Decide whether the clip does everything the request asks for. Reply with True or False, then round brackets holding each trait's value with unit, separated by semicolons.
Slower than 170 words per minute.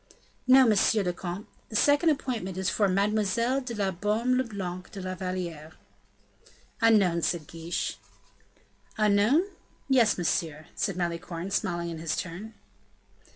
True (140 wpm)